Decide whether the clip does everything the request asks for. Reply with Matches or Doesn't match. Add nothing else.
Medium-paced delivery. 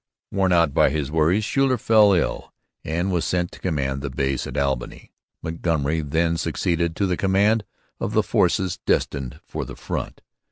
Matches